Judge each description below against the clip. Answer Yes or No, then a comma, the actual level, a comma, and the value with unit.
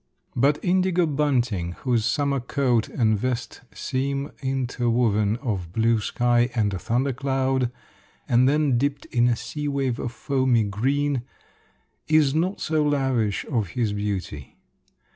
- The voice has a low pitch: Yes, low, 125 Hz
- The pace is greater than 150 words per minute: No, slow, 135 wpm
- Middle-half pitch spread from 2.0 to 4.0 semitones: Yes, average, 3.6 semitones